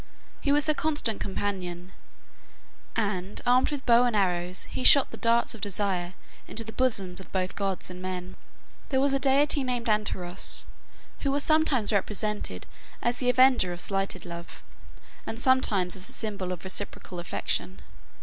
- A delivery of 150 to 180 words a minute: Yes, average, 160 wpm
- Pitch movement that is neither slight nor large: No, wide, 5.7 semitones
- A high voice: Yes, high, 205 Hz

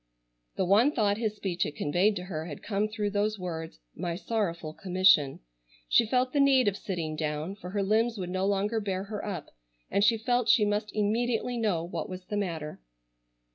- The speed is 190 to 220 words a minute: Yes, average, 195 wpm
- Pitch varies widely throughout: No, average, 3.5 semitones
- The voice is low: No, high, 200 Hz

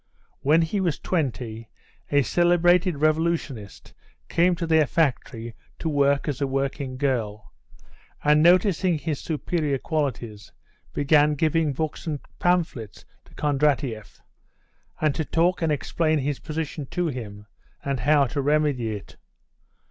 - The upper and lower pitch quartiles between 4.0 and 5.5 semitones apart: No, average, 3.5 semitones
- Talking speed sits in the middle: No, slow, 130 wpm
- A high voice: No, medium, 150 Hz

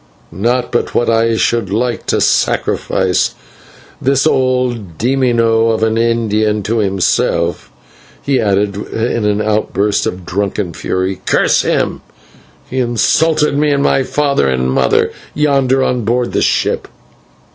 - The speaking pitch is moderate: No, low, 115 Hz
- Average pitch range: Yes, average, 3.8 semitones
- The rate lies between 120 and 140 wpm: Yes, slow, 135 wpm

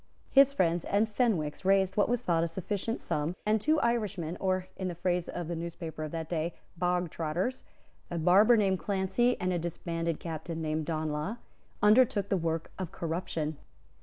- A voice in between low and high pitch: Yes, medium, 175 Hz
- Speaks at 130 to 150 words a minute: No, average, 170 wpm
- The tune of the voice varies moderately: Yes, average, 3.6 semitones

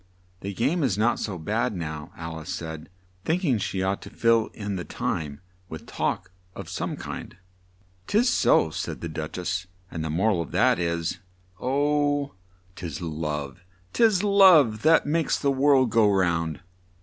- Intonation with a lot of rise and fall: Yes, wide, 8.8 semitones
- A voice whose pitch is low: Yes, very low, 95 Hz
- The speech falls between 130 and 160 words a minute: No, average, 170 wpm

